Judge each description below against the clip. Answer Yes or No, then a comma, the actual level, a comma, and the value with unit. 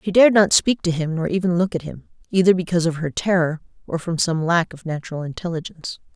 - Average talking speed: No, fast, 225 wpm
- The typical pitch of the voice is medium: Yes, medium, 175 Hz